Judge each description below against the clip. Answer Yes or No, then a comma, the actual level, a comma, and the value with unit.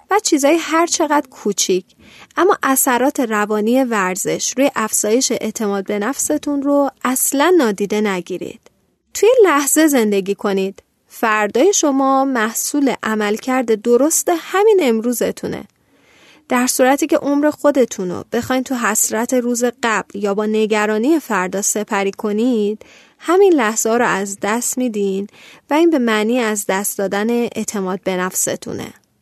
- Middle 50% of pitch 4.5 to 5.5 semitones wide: Yes, average, 5.2 semitones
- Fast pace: No, average, 130 wpm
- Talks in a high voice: Yes, high, 235 Hz